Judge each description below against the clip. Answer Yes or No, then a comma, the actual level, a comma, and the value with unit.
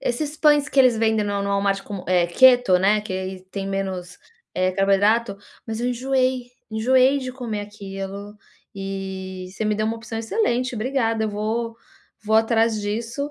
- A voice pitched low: No, high, 215 Hz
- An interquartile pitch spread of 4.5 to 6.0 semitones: No, average, 3.6 semitones